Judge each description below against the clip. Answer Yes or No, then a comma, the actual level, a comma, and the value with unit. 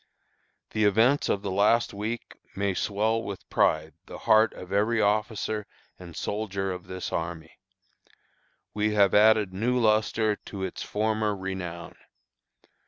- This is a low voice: Yes, low, 105 Hz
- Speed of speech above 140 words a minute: No, slow, 135 wpm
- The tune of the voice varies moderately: No, narrow, 2.3 semitones